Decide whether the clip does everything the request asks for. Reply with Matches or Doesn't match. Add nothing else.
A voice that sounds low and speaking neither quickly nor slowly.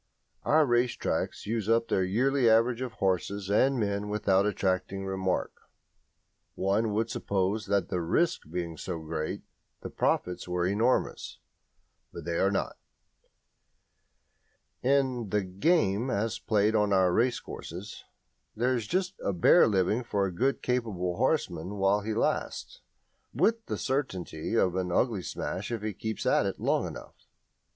Matches